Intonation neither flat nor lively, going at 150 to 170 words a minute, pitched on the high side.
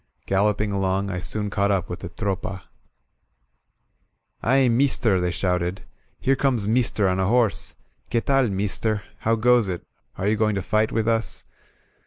No: average, 3.0 semitones; average, 165 wpm; low, 105 Hz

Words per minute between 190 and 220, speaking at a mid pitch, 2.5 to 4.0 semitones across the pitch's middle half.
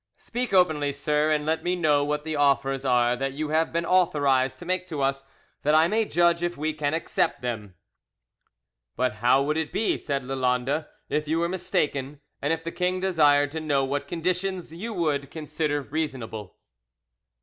No: average, 180 wpm; medium, 150 Hz; average, 3.5 semitones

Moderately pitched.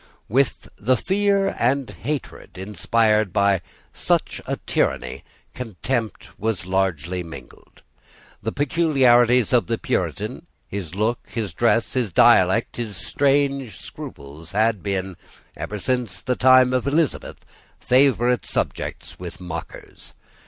No: low, 115 Hz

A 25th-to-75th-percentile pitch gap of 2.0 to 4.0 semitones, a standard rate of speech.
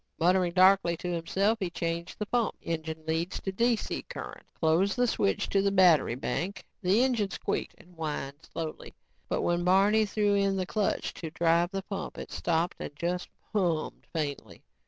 Yes: average, 3.3 semitones; average, 180 wpm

